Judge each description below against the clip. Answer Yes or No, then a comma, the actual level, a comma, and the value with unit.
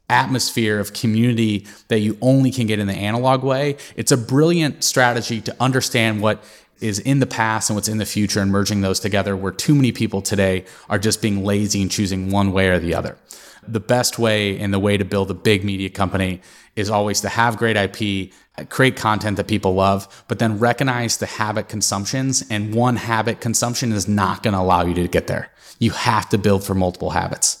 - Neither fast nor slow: No, fast, 210 wpm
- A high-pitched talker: No, low, 105 Hz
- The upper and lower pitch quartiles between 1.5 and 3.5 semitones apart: Yes, average, 2.8 semitones